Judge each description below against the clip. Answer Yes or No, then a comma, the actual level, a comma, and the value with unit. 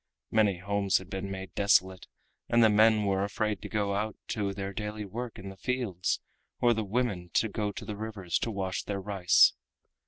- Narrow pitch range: Yes, narrow, 2.0 semitones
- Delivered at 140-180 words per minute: No, average, 195 wpm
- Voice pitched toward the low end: Yes, low, 100 Hz